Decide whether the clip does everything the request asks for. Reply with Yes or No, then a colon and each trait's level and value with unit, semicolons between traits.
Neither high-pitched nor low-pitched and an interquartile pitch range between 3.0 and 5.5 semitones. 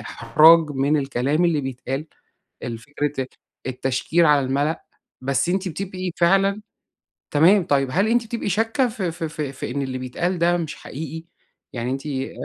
Yes: medium, 155 Hz; average, 4.9 semitones